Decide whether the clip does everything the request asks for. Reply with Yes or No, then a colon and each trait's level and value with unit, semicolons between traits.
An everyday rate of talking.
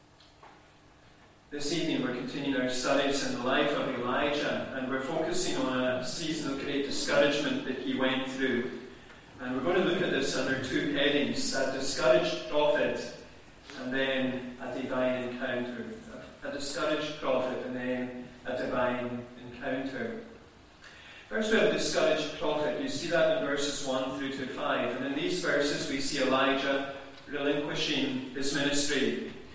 Yes: average, 150 wpm